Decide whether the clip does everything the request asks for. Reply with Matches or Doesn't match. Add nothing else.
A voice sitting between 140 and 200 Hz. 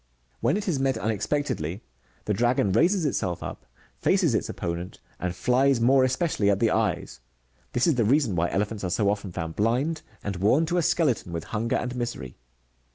Doesn't match